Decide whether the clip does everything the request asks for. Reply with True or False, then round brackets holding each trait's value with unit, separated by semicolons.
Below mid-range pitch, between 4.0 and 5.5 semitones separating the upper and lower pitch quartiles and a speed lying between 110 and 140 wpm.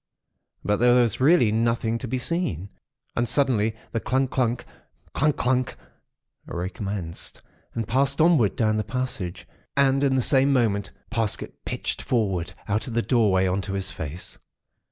False (115 Hz; 4.4 semitones; 150 wpm)